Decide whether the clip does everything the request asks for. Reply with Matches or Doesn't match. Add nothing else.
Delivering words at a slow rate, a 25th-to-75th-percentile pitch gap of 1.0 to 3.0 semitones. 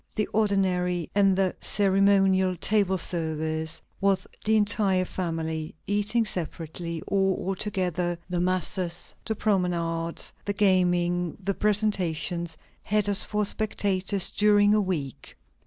Matches